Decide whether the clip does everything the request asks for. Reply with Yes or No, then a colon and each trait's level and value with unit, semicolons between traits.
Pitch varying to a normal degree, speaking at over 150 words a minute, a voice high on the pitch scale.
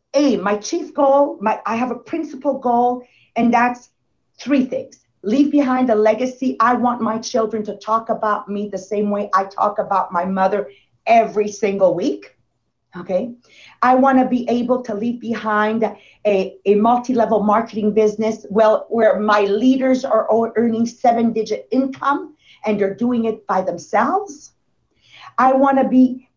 Yes: average, 3.5 semitones; average, 160 wpm; high, 225 Hz